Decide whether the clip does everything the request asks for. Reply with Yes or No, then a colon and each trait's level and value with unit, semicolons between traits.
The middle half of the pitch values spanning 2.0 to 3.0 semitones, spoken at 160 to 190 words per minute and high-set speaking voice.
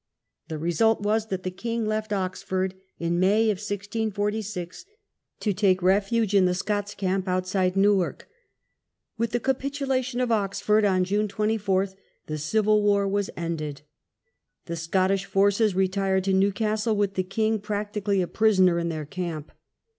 No: narrow, 2.5 semitones; average, 145 wpm; high, 200 Hz